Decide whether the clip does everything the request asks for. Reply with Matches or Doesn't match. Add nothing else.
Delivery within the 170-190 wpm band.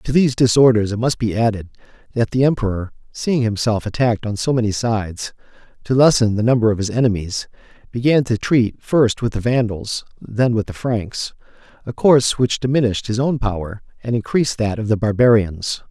Matches